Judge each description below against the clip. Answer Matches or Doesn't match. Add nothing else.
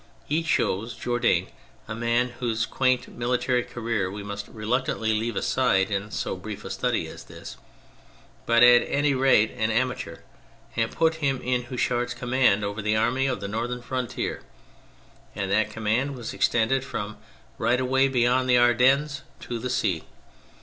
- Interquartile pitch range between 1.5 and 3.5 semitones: Matches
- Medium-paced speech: Matches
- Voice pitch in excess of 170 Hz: Doesn't match